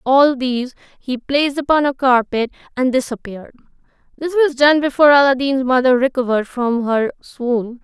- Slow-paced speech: No, average, 145 wpm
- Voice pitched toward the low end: No, very high, 260 Hz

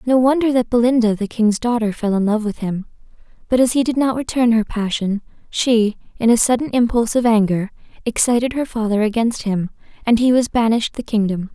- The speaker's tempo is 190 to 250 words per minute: Yes, average, 200 wpm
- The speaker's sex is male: No, female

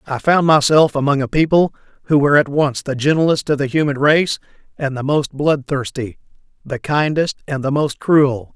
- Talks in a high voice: No, medium, 145 Hz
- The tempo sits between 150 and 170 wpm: No, average, 180 wpm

